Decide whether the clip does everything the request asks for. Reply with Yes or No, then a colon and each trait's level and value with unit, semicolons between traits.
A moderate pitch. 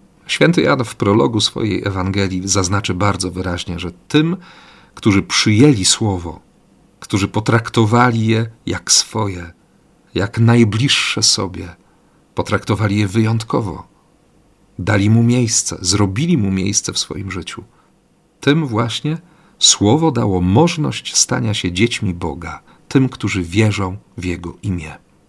No: low, 105 Hz